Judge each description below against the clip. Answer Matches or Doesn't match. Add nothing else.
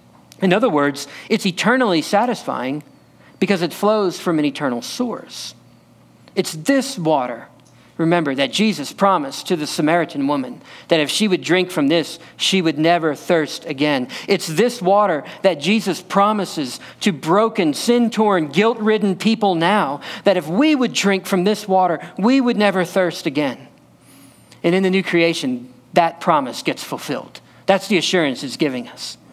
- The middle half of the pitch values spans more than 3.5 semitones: Matches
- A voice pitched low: Doesn't match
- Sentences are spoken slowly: Doesn't match